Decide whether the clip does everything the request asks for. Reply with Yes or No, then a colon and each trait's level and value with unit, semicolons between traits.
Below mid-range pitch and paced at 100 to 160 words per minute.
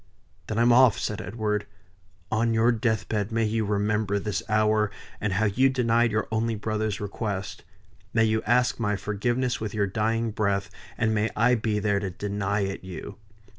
No: low, 110 Hz; average, 170 wpm